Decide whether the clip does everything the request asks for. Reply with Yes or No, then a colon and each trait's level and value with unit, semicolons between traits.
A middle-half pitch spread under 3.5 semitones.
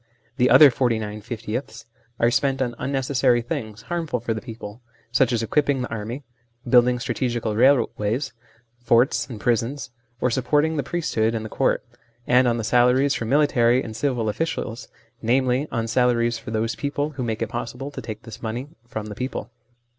Yes: average, 2.8 semitones